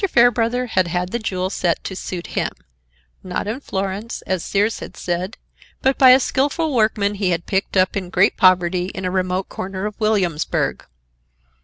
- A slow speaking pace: No, average, 175 wpm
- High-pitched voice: Yes, high, 195 Hz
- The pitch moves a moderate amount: Yes, average, 3.4 semitones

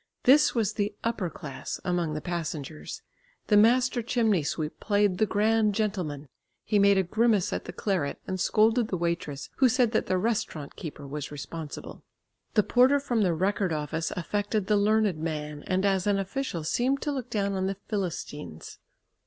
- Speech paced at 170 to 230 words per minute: Yes, average, 175 wpm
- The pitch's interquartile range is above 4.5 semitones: Yes, average, 5.0 semitones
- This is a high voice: Yes, high, 195 Hz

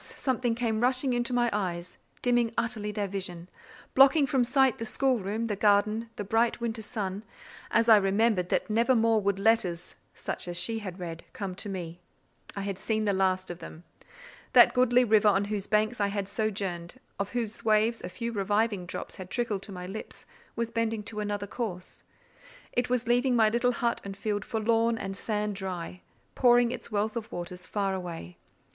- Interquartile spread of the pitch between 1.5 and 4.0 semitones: Yes, average, 3.2 semitones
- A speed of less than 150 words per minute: No, average, 185 wpm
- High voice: Yes, high, 215 Hz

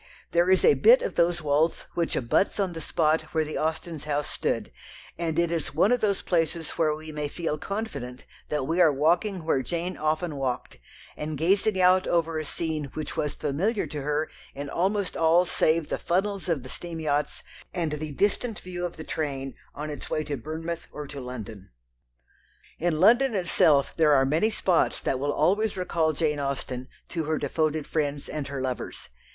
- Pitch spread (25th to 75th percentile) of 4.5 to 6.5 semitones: No, average, 3.1 semitones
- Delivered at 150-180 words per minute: No, average, 190 wpm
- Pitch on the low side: No, medium, 160 Hz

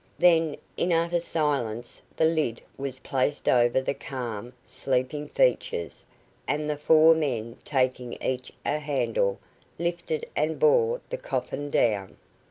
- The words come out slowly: Yes, slow, 130 wpm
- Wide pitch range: No, average, 4.9 semitones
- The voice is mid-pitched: Yes, medium, 150 Hz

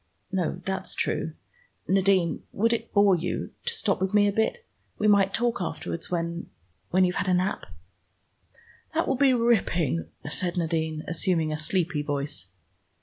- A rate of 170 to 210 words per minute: No, average, 155 wpm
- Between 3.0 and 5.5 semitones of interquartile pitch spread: Yes, average, 3.5 semitones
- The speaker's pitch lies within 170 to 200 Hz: Yes, medium, 185 Hz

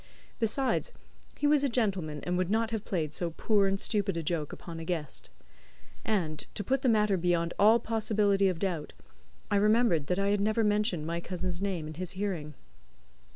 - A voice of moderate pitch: No, high, 195 Hz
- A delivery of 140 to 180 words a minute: No, average, 190 wpm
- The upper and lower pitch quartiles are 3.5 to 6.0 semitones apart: Yes, average, 4.1 semitones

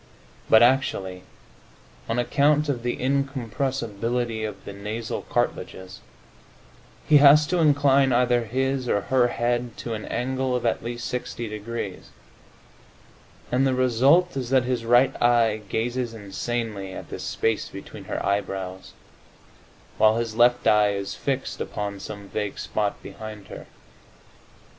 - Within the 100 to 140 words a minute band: Yes, slow, 135 wpm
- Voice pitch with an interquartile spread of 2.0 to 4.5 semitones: Yes, average, 3.4 semitones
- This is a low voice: Yes, low, 120 Hz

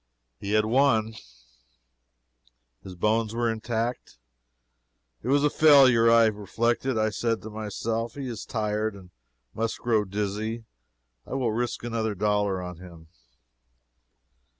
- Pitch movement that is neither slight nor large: No, narrow, 2.1 semitones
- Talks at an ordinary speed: No, slow, 125 wpm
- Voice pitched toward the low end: Yes, low, 110 Hz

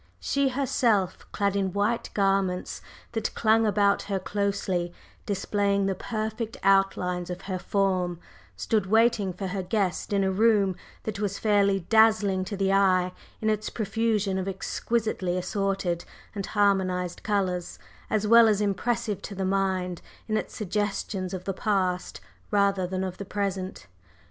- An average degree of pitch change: No, narrow, 2.1 semitones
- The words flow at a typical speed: Yes, average, 150 wpm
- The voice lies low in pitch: No, high, 195 Hz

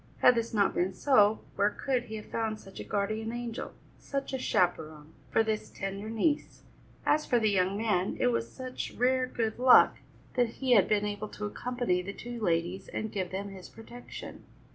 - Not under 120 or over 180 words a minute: No, average, 190 wpm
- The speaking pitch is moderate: No, high, 215 Hz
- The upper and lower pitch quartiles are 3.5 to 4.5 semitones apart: Yes, average, 3.8 semitones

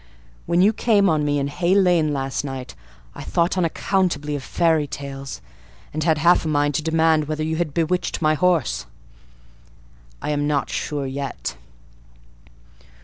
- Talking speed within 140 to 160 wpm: Yes, average, 155 wpm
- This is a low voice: No, medium, 155 Hz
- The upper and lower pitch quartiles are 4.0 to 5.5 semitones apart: No, average, 3.0 semitones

